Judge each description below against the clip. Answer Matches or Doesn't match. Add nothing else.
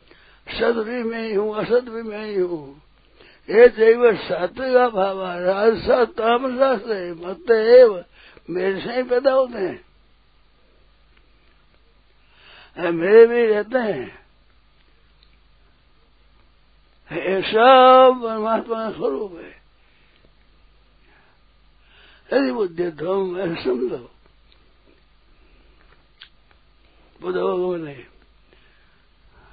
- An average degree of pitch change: Doesn't match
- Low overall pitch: Doesn't match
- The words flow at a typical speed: Doesn't match